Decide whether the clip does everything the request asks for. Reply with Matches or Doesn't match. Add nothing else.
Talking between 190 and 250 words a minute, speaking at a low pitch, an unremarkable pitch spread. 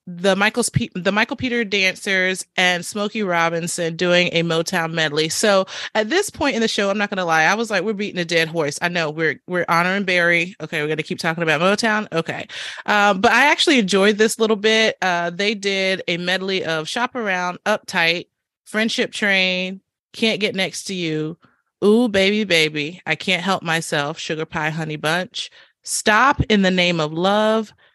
Doesn't match